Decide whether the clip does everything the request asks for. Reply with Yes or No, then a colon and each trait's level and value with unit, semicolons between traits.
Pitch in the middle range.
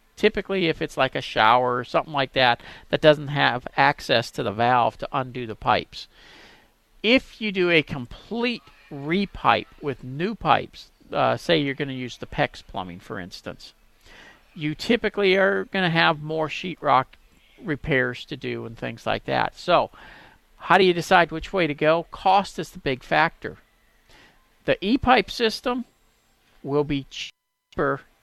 Yes: medium, 155 Hz